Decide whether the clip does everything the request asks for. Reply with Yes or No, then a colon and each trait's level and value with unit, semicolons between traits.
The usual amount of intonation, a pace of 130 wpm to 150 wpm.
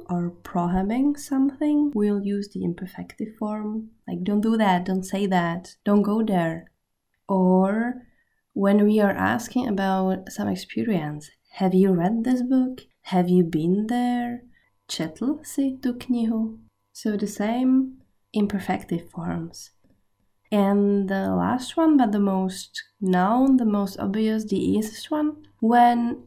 Yes: average, 4.9 semitones; average, 135 wpm